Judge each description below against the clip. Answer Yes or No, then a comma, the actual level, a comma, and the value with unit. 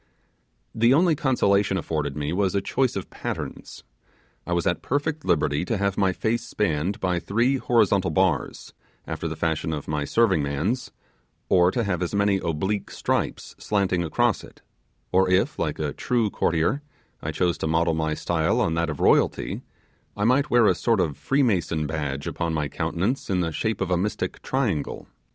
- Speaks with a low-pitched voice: Yes, very low, 95 Hz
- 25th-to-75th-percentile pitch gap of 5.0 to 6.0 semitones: Yes, wide, 5.5 semitones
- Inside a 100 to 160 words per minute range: No, average, 180 wpm